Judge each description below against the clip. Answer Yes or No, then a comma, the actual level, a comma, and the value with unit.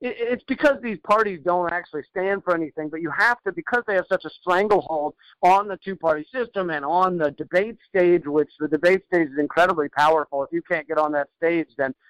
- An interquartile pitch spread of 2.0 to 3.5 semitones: No, average, 4.3 semitones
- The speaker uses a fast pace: Yes, fast, 220 wpm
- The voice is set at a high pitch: No, medium, 175 Hz